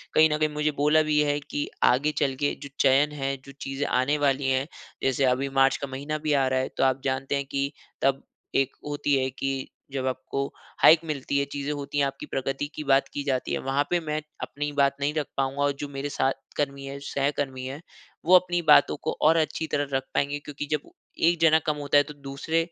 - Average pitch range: No, narrow, 1.6 semitones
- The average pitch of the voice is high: No, medium, 140 Hz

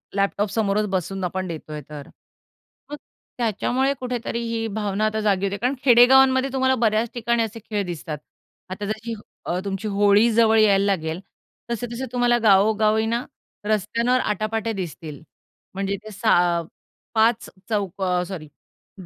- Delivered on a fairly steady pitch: No, average, 3.2 semitones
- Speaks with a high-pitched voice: Yes, high, 215 Hz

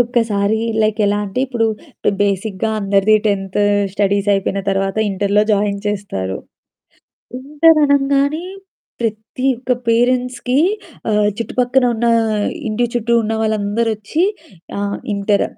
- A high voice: Yes, high, 215 Hz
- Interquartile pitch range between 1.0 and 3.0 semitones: No, average, 3.5 semitones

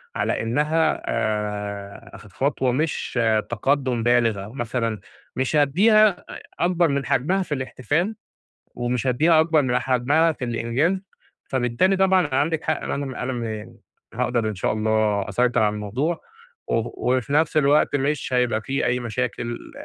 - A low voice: Yes, low, 125 Hz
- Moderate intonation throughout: Yes, average, 4.8 semitones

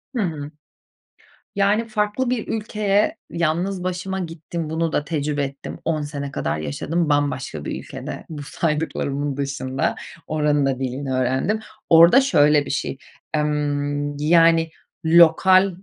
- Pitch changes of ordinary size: Yes, average, 4.1 semitones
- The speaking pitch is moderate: Yes, medium, 155 Hz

